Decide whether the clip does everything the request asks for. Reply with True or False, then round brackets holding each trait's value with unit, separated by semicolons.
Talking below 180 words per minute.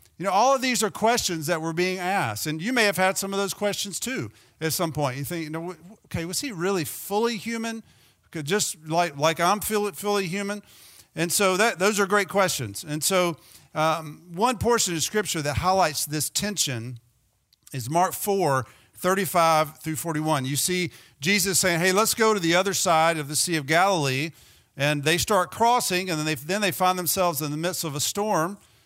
False (200 wpm)